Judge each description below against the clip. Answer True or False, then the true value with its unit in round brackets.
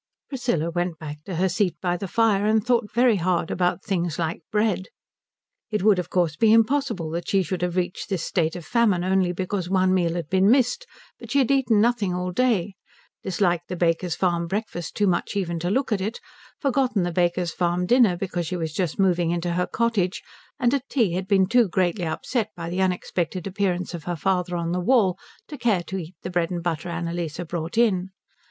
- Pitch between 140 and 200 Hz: True (185 Hz)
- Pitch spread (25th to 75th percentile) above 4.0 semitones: False (3.4 semitones)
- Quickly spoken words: True (210 wpm)